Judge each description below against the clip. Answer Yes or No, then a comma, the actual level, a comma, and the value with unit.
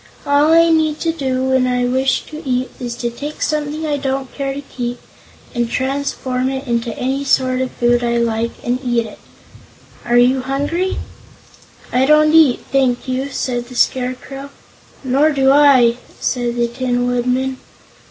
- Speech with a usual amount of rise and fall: No, narrow, 2.3 semitones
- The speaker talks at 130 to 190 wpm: Yes, average, 160 wpm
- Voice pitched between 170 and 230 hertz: No, very high, 260 Hz